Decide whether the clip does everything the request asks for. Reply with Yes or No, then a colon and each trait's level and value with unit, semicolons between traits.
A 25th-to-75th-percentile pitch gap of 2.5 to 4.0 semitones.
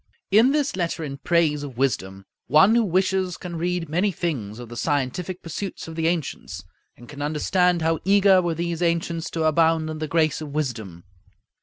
Yes: average, 3.5 semitones